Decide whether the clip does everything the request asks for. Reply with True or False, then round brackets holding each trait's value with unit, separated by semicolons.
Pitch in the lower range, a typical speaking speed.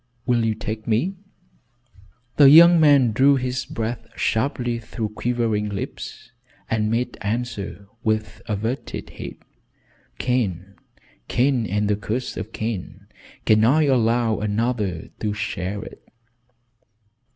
False (115 Hz; 120 wpm)